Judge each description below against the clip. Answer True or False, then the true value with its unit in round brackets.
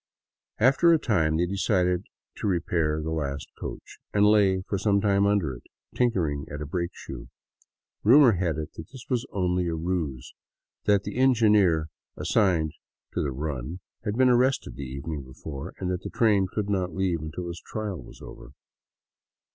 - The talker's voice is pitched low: True (90 Hz)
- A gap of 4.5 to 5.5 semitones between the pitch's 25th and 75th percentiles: True (4.9 semitones)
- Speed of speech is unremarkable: True (170 wpm)